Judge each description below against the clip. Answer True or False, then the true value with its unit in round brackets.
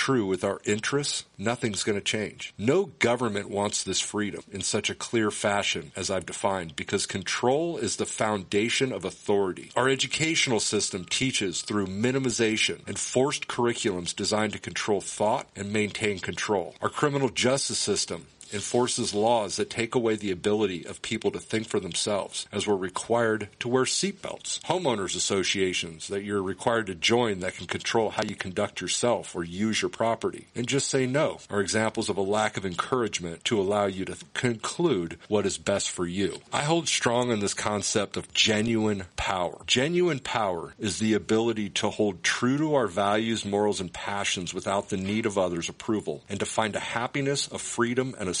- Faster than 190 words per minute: False (180 wpm)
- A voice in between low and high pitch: False (110 Hz)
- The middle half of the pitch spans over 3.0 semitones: True (3.6 semitones)